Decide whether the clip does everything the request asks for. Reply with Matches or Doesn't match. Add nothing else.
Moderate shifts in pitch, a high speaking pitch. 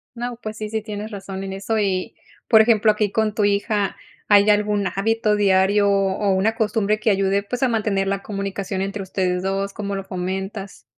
Doesn't match